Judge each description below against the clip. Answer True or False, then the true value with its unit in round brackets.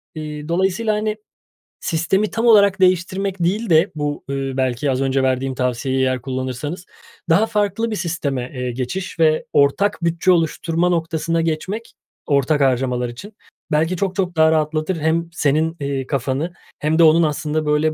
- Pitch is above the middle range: False (160 Hz)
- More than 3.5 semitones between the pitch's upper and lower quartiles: True (5.0 semitones)